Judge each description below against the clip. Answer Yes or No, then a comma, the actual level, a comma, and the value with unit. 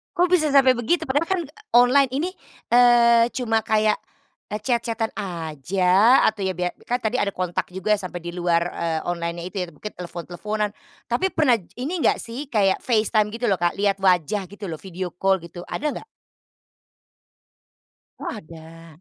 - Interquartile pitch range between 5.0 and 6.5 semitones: Yes, wide, 5.5 semitones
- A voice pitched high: Yes, high, 210 Hz